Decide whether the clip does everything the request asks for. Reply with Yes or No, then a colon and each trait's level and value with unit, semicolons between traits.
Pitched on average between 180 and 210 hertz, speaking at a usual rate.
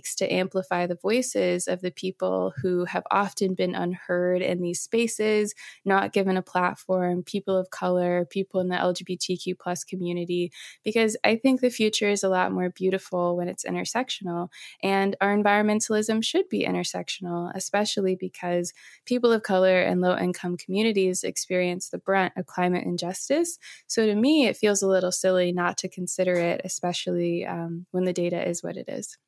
Yes: medium, 185 Hz; average, 170 wpm